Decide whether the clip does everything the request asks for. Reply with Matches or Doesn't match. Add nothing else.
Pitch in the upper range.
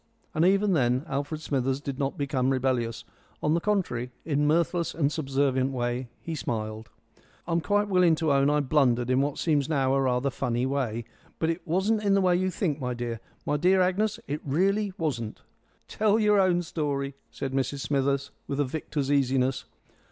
Doesn't match